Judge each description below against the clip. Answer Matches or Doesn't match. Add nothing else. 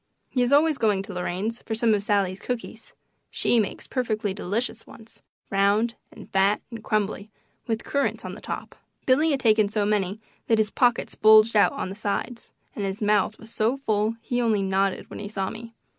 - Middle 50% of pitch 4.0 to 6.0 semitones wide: Doesn't match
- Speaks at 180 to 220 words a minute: Matches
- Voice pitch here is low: Doesn't match